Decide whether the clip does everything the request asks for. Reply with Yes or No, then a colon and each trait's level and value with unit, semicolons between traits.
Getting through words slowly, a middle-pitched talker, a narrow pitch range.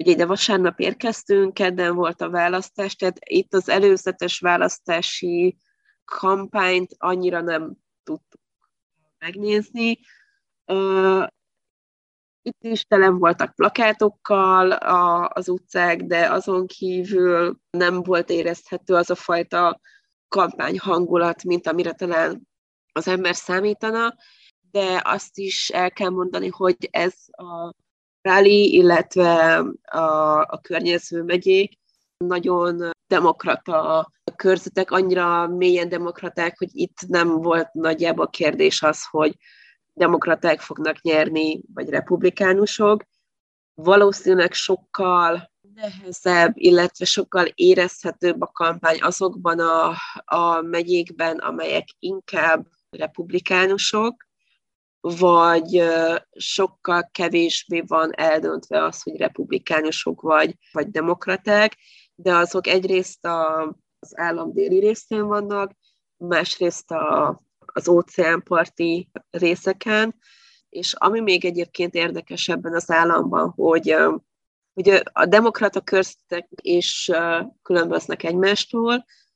Yes: slow, 100 wpm; medium, 180 Hz; narrow, 2.3 semitones